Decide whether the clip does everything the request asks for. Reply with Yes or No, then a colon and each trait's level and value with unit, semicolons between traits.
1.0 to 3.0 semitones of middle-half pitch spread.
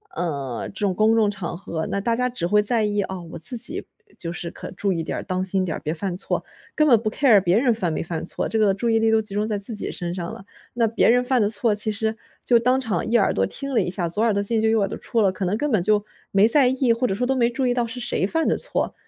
No: average, 3.8 semitones